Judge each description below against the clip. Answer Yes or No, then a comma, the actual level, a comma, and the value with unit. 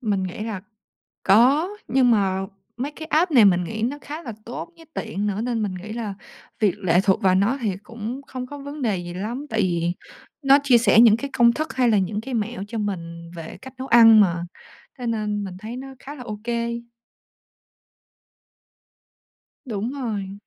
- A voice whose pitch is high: Yes, high, 225 Hz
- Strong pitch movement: No, average, 4.3 semitones